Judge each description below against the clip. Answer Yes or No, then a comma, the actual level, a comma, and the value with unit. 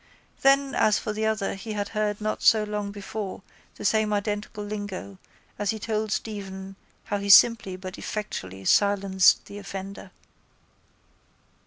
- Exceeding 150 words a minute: No, average, 145 wpm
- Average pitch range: No, narrow, 1.5 semitones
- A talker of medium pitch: No, high, 205 Hz